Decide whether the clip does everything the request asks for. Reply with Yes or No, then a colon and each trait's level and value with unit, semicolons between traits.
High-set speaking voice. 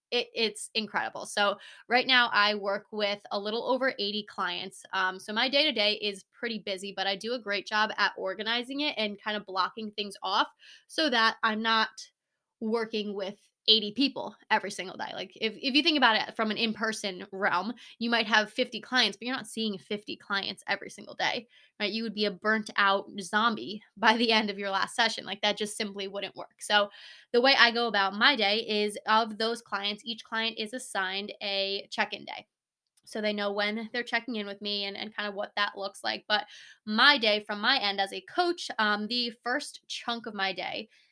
Yes: high, 215 Hz